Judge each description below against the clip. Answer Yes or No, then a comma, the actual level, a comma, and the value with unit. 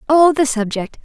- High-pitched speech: Yes, very high, 270 Hz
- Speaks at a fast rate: No, average, 175 wpm